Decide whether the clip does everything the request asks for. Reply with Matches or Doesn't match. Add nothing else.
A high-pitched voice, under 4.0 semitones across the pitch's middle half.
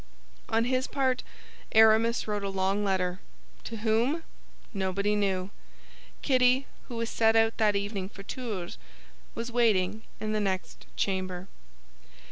Matches